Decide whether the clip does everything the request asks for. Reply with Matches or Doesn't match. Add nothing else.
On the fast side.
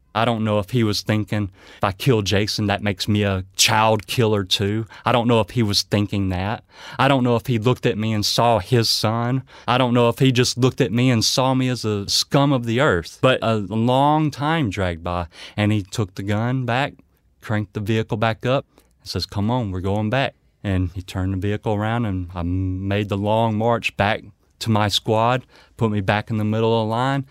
Matches